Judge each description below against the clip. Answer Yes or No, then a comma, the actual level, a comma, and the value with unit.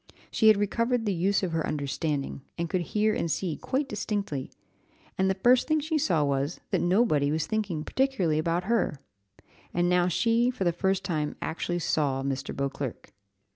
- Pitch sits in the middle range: Yes, medium, 180 Hz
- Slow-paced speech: No, average, 180 wpm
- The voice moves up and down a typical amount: No, wide, 6.0 semitones